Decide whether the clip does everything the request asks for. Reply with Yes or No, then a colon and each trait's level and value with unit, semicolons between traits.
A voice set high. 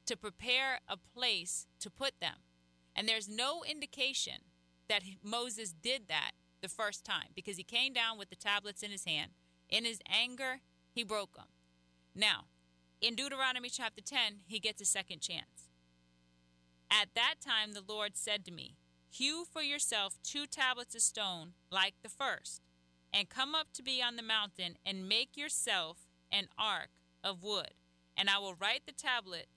Yes: high, 205 Hz